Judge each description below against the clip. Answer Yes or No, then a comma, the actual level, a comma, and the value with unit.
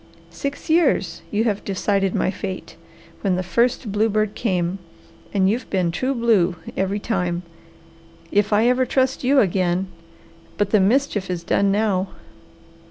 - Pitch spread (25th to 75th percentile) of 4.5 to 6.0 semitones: No, average, 3.8 semitones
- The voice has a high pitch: Yes, high, 205 Hz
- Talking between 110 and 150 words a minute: Yes, average, 145 wpm